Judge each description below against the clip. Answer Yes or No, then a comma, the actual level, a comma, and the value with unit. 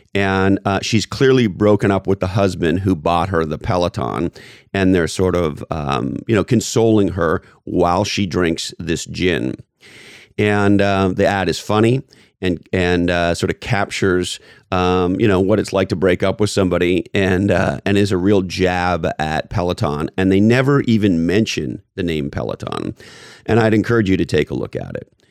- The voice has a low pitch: Yes, very low, 95 Hz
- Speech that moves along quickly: No, average, 185 wpm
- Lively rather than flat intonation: No, narrow, 2.6 semitones